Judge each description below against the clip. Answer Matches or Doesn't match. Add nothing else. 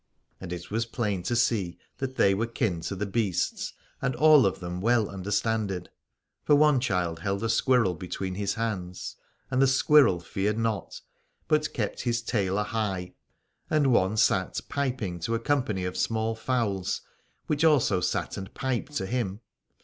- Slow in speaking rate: Doesn't match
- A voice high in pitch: Doesn't match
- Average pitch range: Matches